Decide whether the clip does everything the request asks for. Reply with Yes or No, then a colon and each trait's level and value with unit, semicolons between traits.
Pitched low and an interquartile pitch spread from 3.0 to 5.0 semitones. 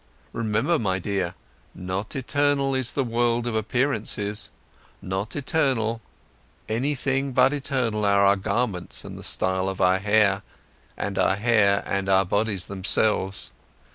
Yes: low, 110 Hz; average, 4.5 semitones